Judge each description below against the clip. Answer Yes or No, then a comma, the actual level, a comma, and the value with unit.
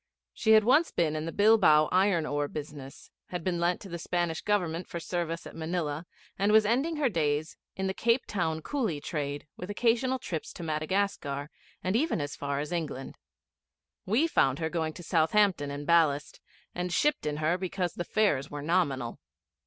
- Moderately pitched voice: Yes, medium, 170 Hz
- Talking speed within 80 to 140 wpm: No, average, 185 wpm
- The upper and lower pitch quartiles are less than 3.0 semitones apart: No, average, 5.0 semitones